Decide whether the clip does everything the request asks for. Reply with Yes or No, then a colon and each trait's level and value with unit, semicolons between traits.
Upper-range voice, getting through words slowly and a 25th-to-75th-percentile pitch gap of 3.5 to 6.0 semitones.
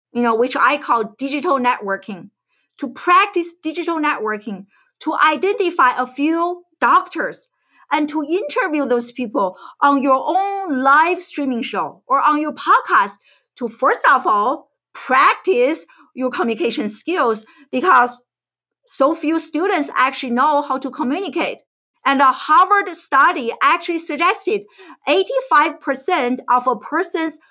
Yes: very high, 300 Hz; slow, 125 wpm; wide, 5.4 semitones